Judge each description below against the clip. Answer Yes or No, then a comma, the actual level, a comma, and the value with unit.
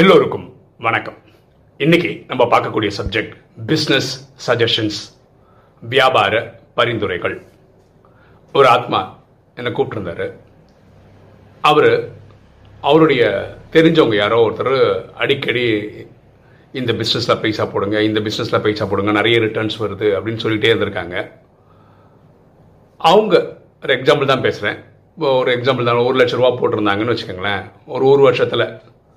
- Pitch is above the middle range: No, low, 130 Hz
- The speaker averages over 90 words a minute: Yes, average, 105 wpm